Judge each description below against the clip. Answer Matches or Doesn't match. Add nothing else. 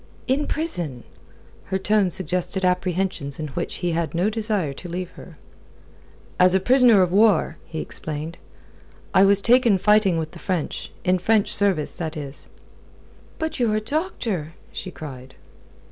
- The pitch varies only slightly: Doesn't match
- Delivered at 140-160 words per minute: Matches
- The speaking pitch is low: Doesn't match